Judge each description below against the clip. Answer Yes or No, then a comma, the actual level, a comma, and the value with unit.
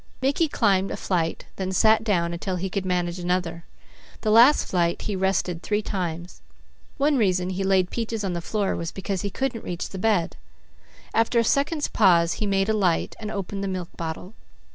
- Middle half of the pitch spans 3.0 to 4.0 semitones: Yes, average, 3.4 semitones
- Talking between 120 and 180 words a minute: No, average, 190 wpm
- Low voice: No, high, 190 Hz